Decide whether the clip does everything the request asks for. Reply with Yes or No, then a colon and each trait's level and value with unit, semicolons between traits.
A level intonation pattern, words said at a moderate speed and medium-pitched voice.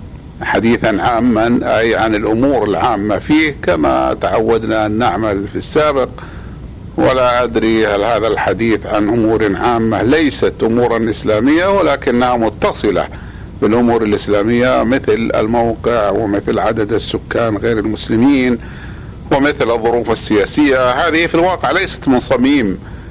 No: narrow, 2.1 semitones; average, 115 wpm; low, 115 Hz